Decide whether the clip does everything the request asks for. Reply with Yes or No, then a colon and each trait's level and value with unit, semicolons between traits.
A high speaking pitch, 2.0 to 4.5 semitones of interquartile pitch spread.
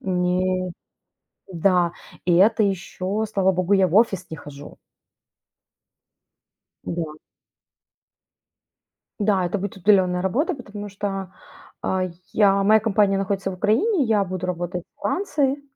Yes: high, 195 Hz; narrow, 2.4 semitones